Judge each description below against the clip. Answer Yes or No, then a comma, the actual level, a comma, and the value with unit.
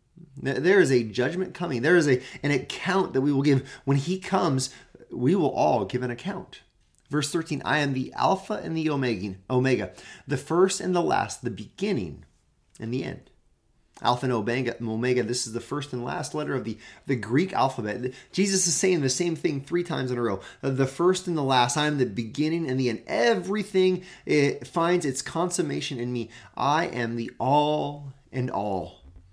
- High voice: No, low, 135 Hz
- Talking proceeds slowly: No, average, 190 wpm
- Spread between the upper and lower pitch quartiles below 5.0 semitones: No, wide, 5.6 semitones